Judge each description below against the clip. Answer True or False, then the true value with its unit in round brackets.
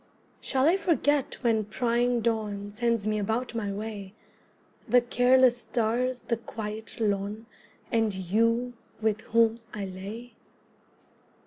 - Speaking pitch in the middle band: False (225 Hz)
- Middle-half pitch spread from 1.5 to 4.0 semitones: True (2.6 semitones)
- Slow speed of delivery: True (120 wpm)